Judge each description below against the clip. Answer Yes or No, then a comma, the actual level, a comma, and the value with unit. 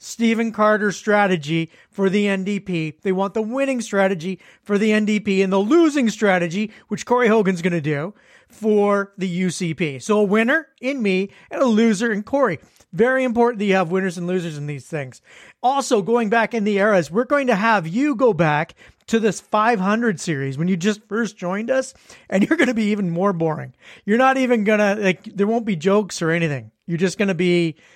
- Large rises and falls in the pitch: No, average, 3.7 semitones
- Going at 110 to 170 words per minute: No, average, 200 wpm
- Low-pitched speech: No, high, 205 Hz